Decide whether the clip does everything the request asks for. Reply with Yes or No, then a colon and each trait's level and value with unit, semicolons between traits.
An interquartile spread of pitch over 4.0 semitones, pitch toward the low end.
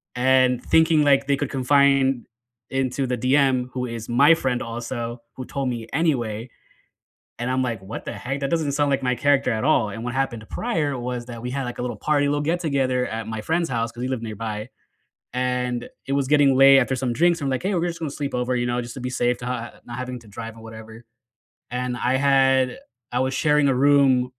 No: narrow, 2.5 semitones; low, 130 Hz